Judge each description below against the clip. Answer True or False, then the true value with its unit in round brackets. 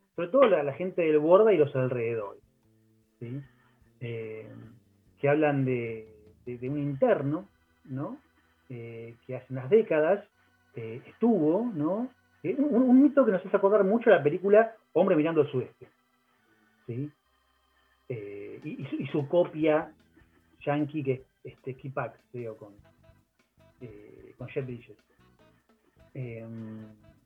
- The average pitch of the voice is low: True (130 Hz)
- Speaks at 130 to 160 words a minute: True (135 wpm)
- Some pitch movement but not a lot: False (5.7 semitones)